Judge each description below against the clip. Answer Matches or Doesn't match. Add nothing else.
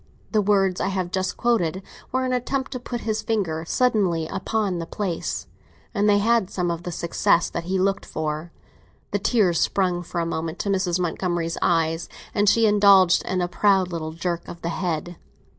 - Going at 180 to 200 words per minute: Matches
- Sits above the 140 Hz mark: Matches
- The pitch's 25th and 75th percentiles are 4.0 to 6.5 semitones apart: Doesn't match